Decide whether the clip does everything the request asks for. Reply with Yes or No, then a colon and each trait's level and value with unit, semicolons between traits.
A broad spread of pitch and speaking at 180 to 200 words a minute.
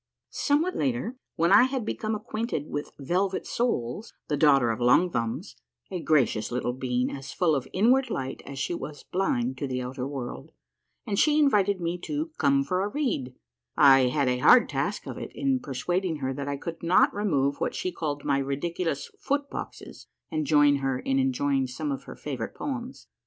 Yes: wide, 7.3 semitones; average, 195 wpm